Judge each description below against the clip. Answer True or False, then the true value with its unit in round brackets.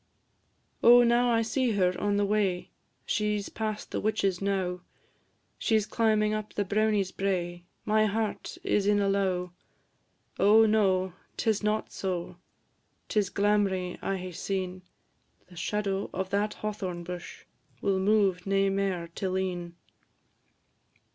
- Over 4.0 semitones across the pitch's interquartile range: False (2.4 semitones)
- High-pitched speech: True (200 Hz)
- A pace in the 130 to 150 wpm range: True (140 wpm)